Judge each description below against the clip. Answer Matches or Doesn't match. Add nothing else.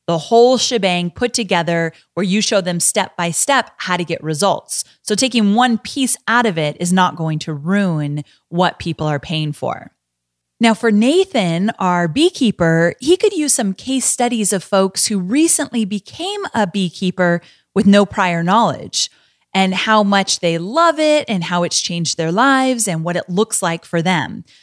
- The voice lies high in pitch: Matches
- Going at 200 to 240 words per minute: Doesn't match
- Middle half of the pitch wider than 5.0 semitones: Matches